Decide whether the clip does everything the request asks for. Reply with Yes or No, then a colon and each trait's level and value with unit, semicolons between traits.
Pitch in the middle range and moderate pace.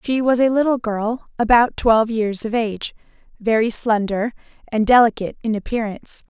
No: high, 225 Hz; average, 150 wpm